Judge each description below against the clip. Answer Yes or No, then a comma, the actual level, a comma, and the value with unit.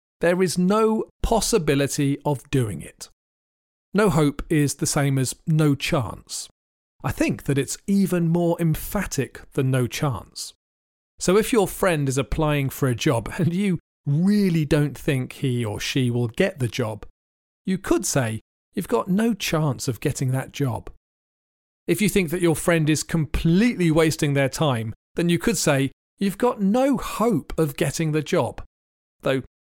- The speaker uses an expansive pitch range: Yes, wide, 5.9 semitones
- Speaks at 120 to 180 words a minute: Yes, average, 165 wpm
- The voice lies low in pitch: No, medium, 150 Hz